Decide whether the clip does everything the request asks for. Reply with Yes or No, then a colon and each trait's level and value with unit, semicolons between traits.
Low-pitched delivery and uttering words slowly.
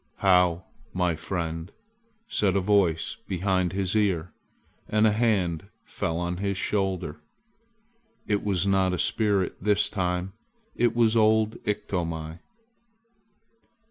Yes: very low, 95 Hz; slow, 115 wpm